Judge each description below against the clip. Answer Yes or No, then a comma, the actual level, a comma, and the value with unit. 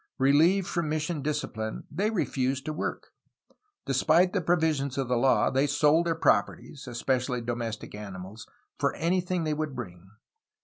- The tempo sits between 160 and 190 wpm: No, average, 145 wpm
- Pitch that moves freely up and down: No, average, 4.9 semitones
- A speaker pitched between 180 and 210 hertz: No, medium, 140 Hz